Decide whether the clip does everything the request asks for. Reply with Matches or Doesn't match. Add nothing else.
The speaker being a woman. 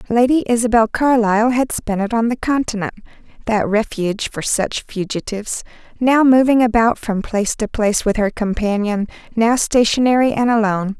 Matches